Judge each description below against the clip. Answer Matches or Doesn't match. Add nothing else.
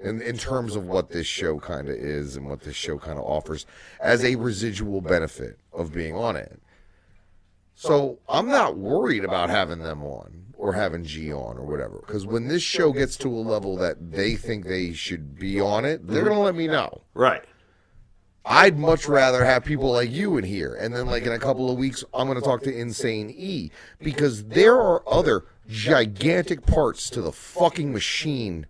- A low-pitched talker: Matches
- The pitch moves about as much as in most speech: Doesn't match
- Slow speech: Doesn't match